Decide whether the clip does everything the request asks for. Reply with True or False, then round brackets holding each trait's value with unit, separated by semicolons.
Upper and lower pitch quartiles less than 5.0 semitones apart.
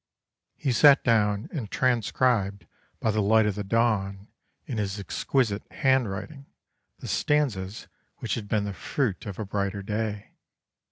True (3.5 semitones)